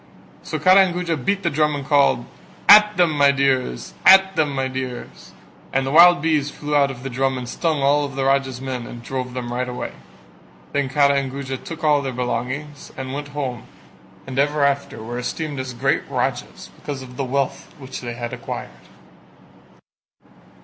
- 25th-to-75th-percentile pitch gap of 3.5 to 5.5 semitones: No, narrow, 2.5 semitones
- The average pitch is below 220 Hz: Yes, medium, 140 Hz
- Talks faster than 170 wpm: Yes, average, 185 wpm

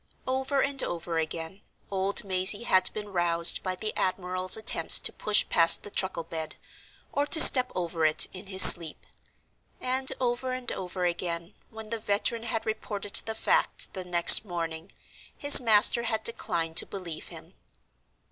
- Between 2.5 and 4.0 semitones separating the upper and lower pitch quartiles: No, average, 4.6 semitones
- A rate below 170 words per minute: Yes, average, 160 wpm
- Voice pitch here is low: No, high, 190 Hz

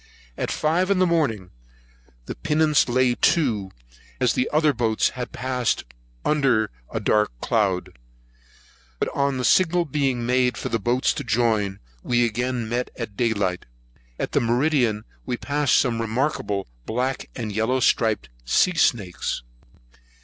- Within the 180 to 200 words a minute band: No, average, 145 wpm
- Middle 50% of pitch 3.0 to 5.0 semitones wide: Yes, average, 3.9 semitones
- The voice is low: Yes, low, 120 Hz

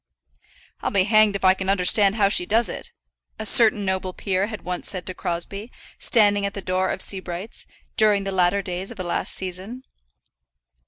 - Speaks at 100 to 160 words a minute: No, average, 190 wpm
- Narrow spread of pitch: Yes, narrow, 2.1 semitones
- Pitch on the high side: Yes, high, 195 Hz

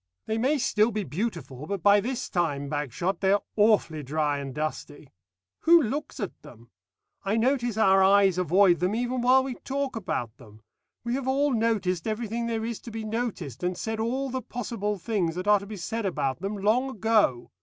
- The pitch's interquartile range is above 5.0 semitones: Yes, wide, 5.4 semitones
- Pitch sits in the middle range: No, high, 205 Hz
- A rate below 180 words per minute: No, average, 195 wpm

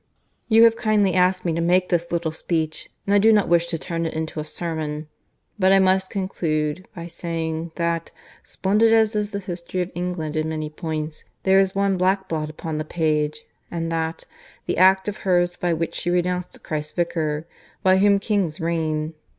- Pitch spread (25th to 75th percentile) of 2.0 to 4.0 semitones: Yes, average, 3.0 semitones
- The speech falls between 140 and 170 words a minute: No, average, 190 wpm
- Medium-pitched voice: Yes, medium, 170 Hz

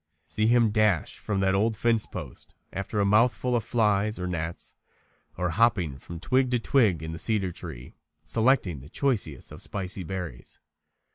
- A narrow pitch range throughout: No, average, 4.6 semitones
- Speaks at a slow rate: No, average, 170 wpm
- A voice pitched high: No, low, 100 Hz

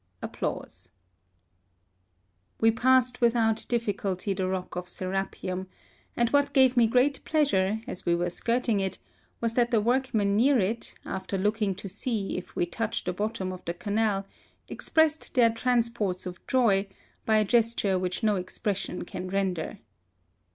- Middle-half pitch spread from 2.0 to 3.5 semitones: No, average, 4.1 semitones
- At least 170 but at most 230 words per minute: No, average, 150 wpm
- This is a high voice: Yes, high, 215 Hz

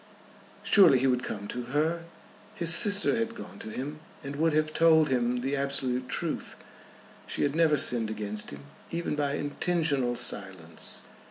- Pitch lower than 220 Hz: Yes, medium, 140 Hz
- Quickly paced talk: No, average, 160 wpm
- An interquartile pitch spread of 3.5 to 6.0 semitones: Yes, average, 4.7 semitones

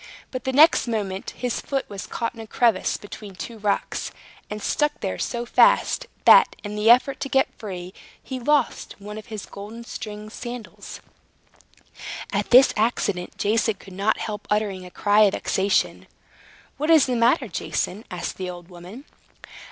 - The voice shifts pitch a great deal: No, average, 3.5 semitones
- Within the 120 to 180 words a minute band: Yes, average, 165 wpm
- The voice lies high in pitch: Yes, high, 215 Hz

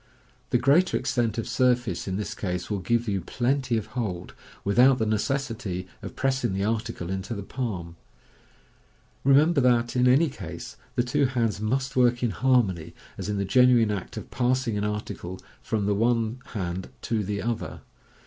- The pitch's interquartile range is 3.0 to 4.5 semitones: Yes, average, 4.0 semitones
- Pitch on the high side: No, low, 115 Hz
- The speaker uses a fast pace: No, average, 175 wpm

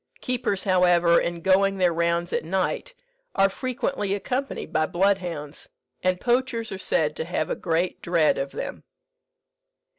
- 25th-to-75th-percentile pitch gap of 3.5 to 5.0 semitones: No, average, 3.0 semitones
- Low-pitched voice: No, medium, 185 Hz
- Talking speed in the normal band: Yes, average, 145 wpm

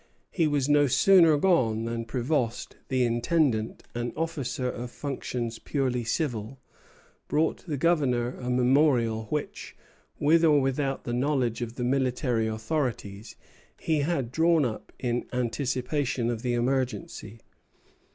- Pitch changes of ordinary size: Yes, average, 3.7 semitones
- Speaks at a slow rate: Yes, slow, 130 wpm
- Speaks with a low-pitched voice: Yes, low, 130 Hz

